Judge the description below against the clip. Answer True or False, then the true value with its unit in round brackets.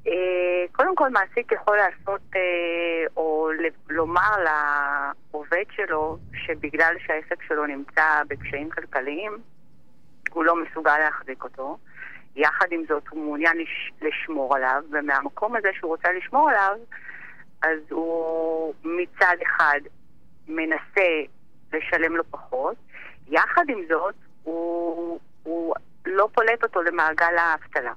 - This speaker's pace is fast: False (110 wpm)